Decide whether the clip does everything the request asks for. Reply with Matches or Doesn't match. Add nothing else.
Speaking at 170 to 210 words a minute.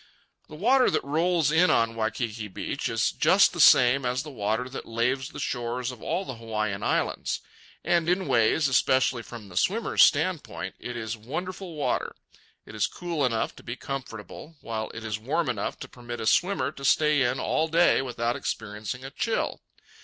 Matches